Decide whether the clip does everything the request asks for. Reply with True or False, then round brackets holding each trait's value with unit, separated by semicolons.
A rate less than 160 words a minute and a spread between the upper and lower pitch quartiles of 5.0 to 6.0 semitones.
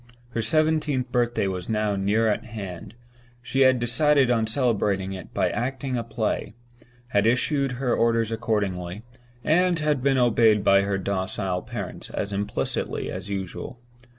False (150 wpm; 4.1 semitones)